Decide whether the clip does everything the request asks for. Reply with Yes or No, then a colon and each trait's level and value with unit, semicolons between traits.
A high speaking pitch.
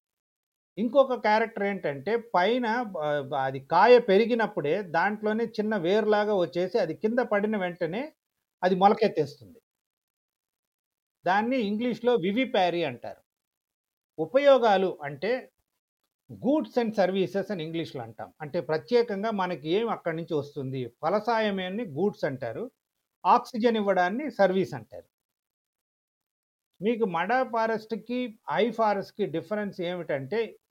Yes: high, 205 Hz